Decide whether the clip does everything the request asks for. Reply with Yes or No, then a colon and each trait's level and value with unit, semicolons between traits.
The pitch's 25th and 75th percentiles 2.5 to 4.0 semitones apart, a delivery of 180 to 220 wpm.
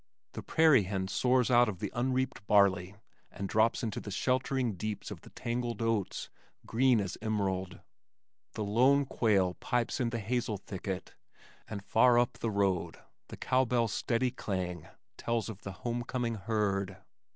No: average, 3.7 semitones; average, 155 wpm